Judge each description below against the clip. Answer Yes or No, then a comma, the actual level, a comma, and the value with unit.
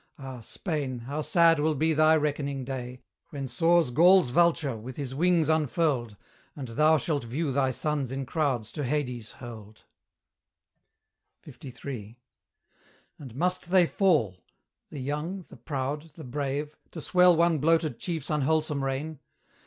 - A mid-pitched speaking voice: Yes, medium, 145 Hz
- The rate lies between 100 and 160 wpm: Yes, average, 140 wpm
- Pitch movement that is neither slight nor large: Yes, average, 3.6 semitones